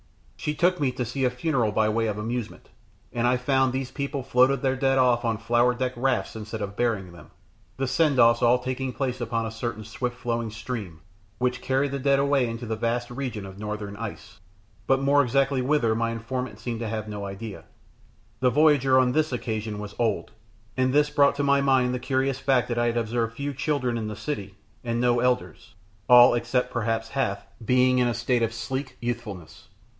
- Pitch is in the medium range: No, low, 120 Hz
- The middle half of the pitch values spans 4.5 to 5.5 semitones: No, average, 2.7 semitones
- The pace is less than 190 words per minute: No, fast, 205 wpm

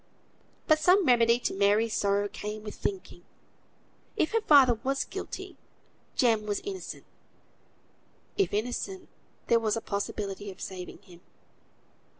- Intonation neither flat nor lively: No, wide, 6.5 semitones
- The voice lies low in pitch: No, high, 225 Hz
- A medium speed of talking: No, slow, 130 wpm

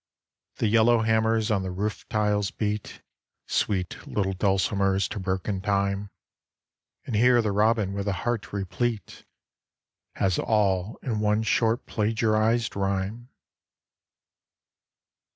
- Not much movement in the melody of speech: Yes, narrow, 2.2 semitones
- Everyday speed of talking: No, slow, 110 wpm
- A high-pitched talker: No, low, 105 Hz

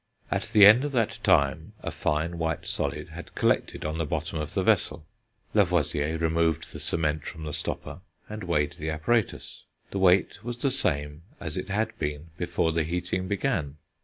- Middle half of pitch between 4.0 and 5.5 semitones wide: Yes, average, 4.4 semitones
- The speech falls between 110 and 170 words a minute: No, average, 180 wpm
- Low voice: Yes, very low, 85 Hz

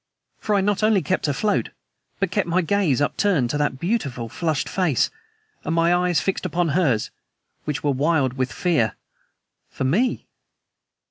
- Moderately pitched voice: Yes, medium, 165 Hz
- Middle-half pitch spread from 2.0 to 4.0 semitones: No, average, 5.3 semitones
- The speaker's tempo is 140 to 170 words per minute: Yes, average, 155 wpm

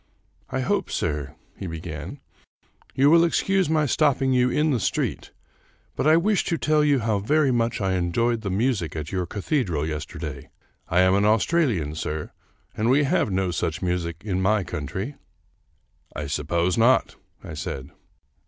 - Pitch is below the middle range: Yes, low, 105 Hz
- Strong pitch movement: Yes, wide, 8.3 semitones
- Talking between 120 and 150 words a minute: No, average, 170 wpm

